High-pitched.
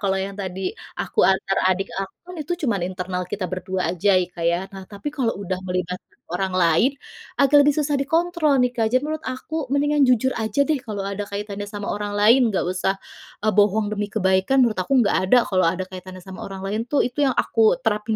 Yes: high, 205 Hz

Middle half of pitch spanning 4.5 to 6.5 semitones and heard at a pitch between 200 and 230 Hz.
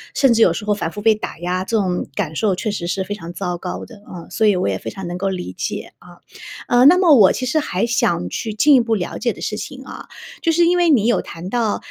Yes: average, 5.2 semitones; high, 210 Hz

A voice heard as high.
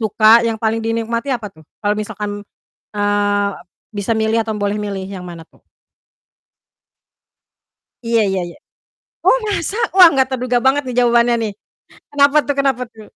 Yes: high, 225 Hz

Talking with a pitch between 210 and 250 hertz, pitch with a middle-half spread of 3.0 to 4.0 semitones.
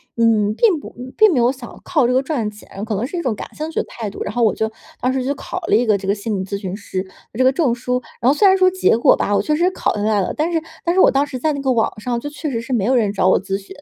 No: high, 245 Hz; wide, 5.6 semitones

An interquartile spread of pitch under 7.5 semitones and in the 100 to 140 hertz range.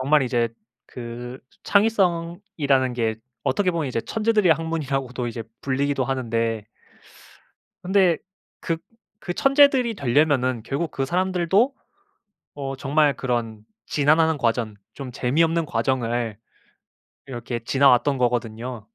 Yes: wide, 5.5 semitones; low, 135 Hz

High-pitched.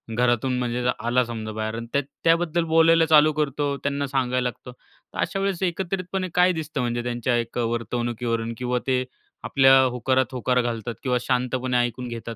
No: low, 125 Hz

